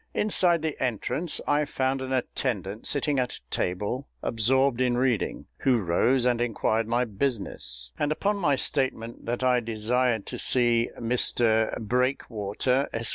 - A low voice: Yes, low, 125 Hz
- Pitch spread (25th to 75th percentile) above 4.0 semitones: No, average, 2.9 semitones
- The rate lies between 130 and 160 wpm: Yes, average, 145 wpm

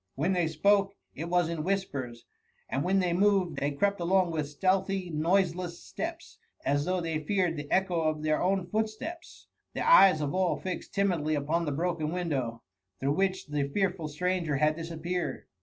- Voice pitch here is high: No, medium, 170 Hz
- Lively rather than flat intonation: No, average, 3.7 semitones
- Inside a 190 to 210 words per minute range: No, average, 175 wpm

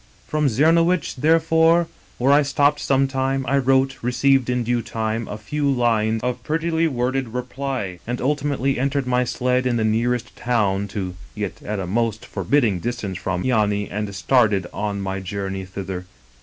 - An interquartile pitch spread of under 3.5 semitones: No, average, 4.5 semitones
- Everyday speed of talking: Yes, average, 170 wpm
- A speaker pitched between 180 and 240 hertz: No, low, 125 Hz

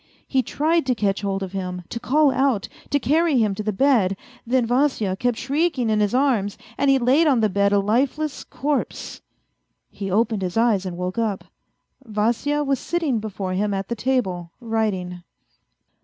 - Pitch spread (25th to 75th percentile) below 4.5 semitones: No, average, 5.3 semitones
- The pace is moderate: Yes, average, 180 wpm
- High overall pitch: Yes, high, 225 Hz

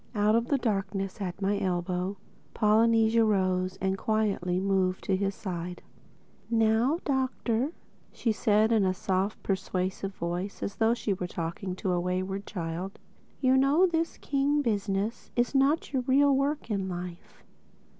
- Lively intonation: No, average, 3.9 semitones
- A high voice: Yes, high, 200 Hz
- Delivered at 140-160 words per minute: Yes, average, 155 wpm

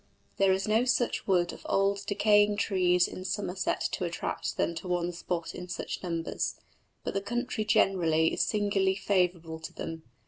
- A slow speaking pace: No, average, 170 wpm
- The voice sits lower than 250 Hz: Yes, high, 190 Hz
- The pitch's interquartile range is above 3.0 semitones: No, average, 2.7 semitones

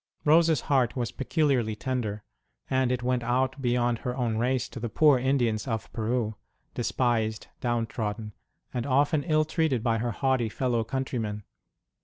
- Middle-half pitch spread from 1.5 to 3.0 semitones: Yes, average, 2.7 semitones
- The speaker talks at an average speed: Yes, average, 160 wpm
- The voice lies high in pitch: No, low, 125 Hz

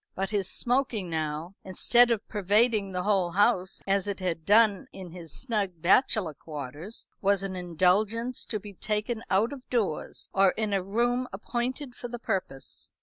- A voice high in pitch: Yes, high, 200 Hz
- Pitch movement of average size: Yes, average, 4.2 semitones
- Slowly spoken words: No, average, 165 wpm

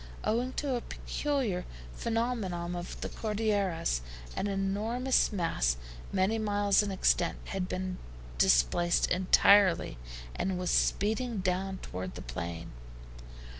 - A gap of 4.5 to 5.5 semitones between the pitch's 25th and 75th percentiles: No, average, 3.8 semitones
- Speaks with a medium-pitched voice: No, high, 195 Hz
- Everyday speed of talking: No, slow, 115 wpm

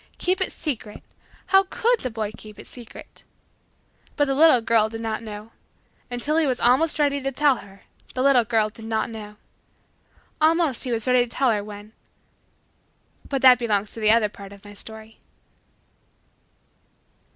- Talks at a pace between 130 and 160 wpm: No, average, 170 wpm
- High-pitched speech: Yes, high, 230 Hz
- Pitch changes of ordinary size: Yes, average, 4.3 semitones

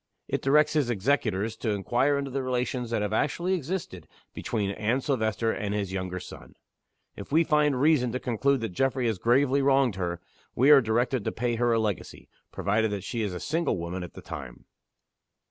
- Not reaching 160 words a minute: No, average, 195 wpm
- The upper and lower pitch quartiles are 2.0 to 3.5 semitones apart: No, average, 5.0 semitones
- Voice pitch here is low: Yes, low, 120 Hz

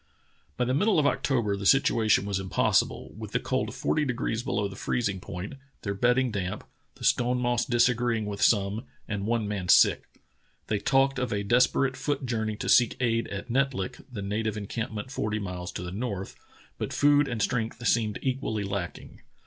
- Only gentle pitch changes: No, average, 3.7 semitones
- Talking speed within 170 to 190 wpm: Yes, average, 185 wpm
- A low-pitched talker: Yes, low, 115 Hz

